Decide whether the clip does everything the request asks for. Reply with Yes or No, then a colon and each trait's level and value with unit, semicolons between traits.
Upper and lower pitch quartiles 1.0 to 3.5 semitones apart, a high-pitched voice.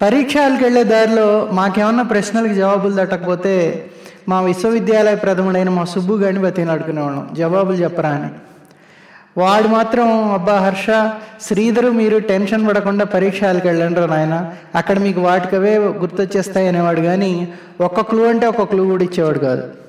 Yes: average, 3.2 semitones; high, 195 Hz